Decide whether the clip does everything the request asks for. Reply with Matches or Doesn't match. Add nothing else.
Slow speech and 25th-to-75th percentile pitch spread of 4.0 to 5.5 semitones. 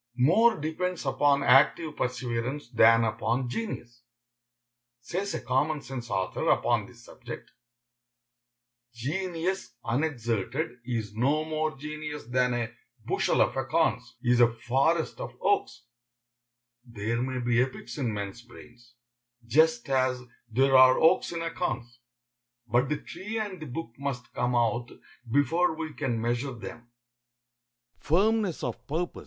Matches